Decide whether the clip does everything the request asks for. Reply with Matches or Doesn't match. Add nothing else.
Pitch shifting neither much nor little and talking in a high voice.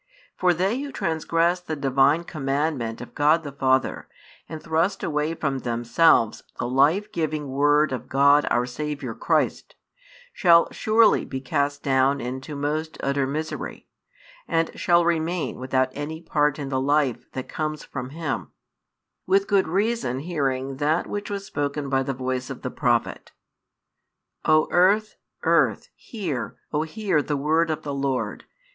Doesn't match